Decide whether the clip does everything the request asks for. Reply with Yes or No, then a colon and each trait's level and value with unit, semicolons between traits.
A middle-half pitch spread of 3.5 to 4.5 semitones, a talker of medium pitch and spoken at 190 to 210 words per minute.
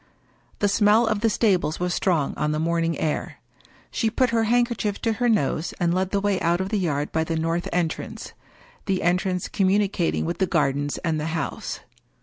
Yes: average, 4.1 semitones; medium, 180 Hz; average, 200 wpm